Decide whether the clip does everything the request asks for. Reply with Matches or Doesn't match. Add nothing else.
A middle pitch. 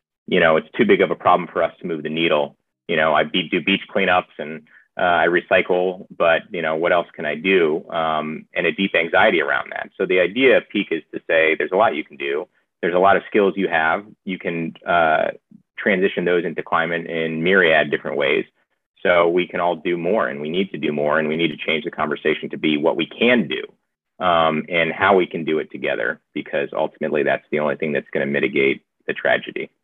Doesn't match